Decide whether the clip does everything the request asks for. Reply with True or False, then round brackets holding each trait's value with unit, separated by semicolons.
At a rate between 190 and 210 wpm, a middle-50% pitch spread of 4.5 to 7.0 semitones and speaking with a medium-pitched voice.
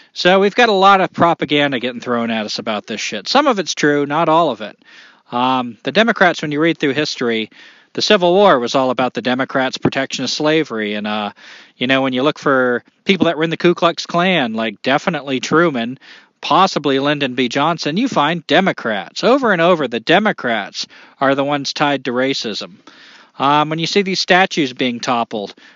True (200 wpm; 5.1 semitones; 145 Hz)